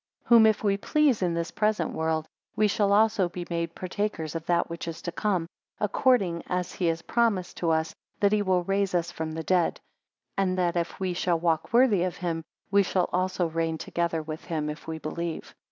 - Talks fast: Yes, fast, 210 wpm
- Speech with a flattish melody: No, average, 3.4 semitones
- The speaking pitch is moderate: Yes, medium, 175 Hz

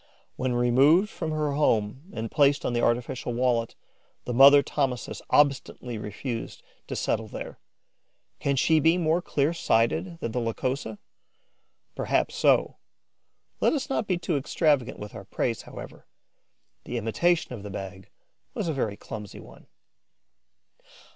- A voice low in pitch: Yes, low, 130 Hz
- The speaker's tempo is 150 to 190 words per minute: No, average, 140 wpm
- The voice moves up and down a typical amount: Yes, average, 5.0 semitones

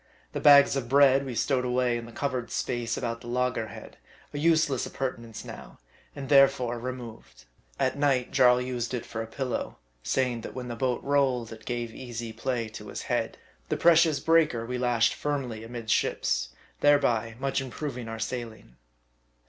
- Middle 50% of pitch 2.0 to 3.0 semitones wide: Yes, average, 2.7 semitones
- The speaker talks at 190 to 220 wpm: No, average, 170 wpm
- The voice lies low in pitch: Yes, low, 125 Hz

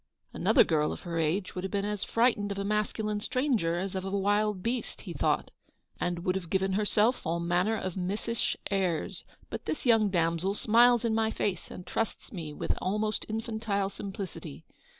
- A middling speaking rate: Yes, average, 190 wpm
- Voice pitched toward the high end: Yes, high, 200 Hz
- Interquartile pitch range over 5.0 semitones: No, average, 3.1 semitones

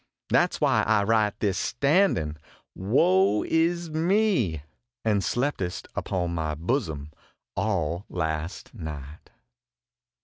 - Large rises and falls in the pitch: Yes, wide, 8.0 semitones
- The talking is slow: Yes, slow, 110 wpm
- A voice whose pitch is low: Yes, low, 100 Hz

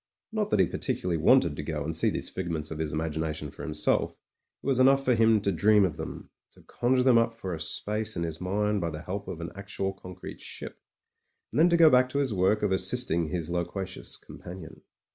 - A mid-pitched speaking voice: No, very low, 95 Hz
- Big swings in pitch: Yes, wide, 5.9 semitones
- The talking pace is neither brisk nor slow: No, fast, 230 wpm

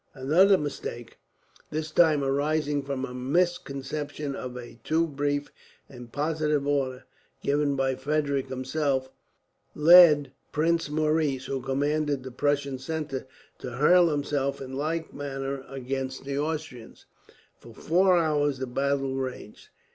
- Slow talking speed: Yes, slow, 125 wpm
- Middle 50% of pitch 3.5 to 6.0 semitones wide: No, narrow, 2.4 semitones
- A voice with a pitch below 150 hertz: Yes, medium, 140 Hz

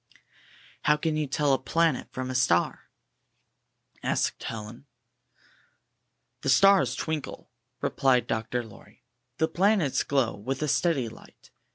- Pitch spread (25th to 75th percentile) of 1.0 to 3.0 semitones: No, average, 4.2 semitones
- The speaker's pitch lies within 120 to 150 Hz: Yes, low, 135 Hz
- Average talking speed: No, slow, 125 wpm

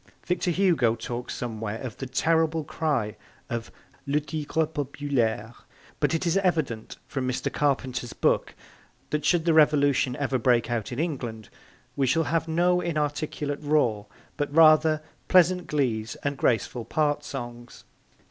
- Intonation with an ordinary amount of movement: Yes, average, 4.7 semitones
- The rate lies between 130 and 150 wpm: Yes, average, 140 wpm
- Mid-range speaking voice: Yes, medium, 145 Hz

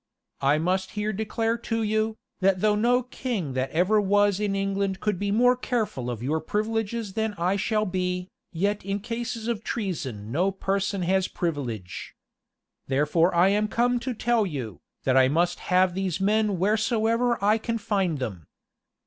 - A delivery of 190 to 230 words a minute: No, average, 165 wpm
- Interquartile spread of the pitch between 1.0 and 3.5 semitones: No, average, 3.9 semitones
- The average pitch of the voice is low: No, high, 200 Hz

